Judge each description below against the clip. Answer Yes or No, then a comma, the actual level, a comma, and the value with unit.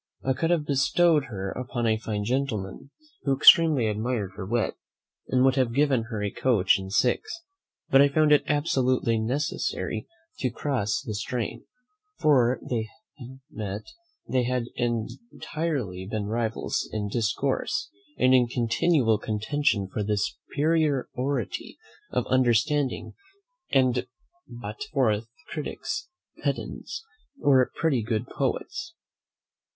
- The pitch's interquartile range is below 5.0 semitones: Yes, average, 4.6 semitones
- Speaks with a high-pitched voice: No, low, 125 Hz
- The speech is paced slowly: Yes, slow, 125 wpm